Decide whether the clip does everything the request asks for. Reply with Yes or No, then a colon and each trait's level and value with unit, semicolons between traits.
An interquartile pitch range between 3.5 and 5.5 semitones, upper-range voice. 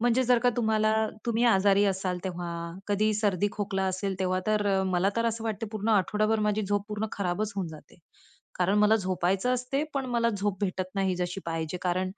No: average, 2.8 semitones; high, 205 Hz